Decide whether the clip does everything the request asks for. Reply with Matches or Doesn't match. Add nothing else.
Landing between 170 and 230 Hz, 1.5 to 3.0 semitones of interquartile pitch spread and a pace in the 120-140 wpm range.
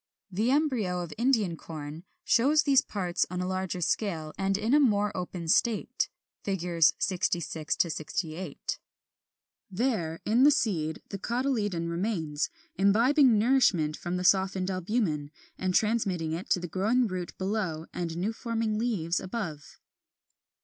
Doesn't match